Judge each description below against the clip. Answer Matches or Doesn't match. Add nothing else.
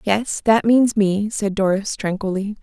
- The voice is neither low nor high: Doesn't match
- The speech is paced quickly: Doesn't match